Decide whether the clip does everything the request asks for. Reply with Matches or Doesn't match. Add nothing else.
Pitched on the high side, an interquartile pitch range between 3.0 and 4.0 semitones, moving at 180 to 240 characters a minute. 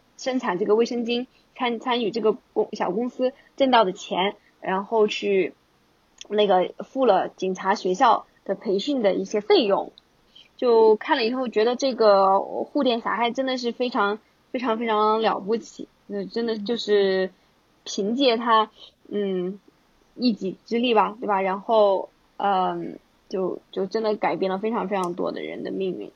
Matches